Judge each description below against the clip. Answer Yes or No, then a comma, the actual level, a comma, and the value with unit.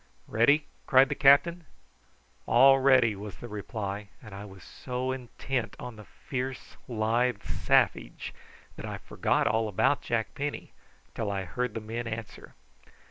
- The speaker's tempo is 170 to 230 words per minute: No, average, 145 wpm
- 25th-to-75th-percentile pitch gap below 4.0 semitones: Yes, average, 3.6 semitones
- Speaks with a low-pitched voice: Yes, low, 120 Hz